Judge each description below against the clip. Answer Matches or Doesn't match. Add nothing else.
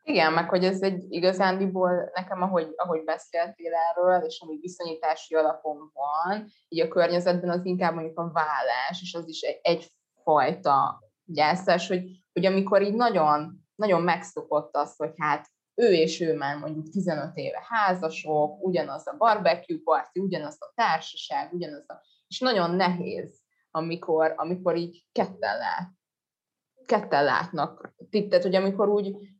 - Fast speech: Doesn't match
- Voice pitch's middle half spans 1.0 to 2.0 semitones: Doesn't match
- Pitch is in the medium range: Matches